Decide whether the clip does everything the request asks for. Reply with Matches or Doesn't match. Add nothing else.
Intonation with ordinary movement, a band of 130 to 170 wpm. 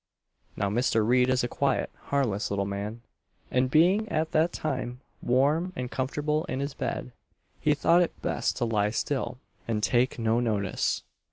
Matches